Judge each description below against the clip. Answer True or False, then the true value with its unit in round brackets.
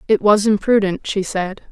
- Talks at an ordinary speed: True (175 wpm)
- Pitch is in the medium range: False (200 Hz)